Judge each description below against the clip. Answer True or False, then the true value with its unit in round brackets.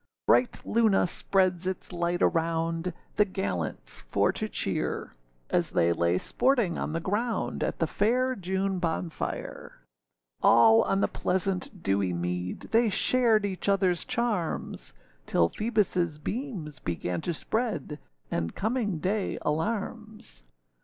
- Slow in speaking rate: True (125 wpm)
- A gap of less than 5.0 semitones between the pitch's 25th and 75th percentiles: False (5.6 semitones)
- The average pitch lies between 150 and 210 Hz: True (185 Hz)